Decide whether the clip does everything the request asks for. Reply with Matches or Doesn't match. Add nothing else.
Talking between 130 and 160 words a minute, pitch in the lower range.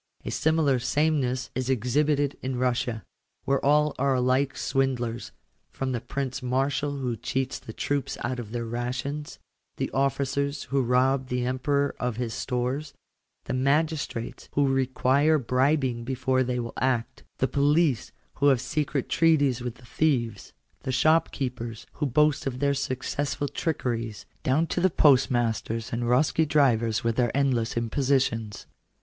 Matches